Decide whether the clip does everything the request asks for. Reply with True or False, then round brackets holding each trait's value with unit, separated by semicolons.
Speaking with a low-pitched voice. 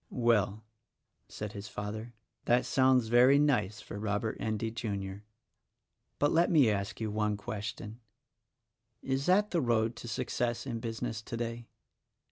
True (115 Hz)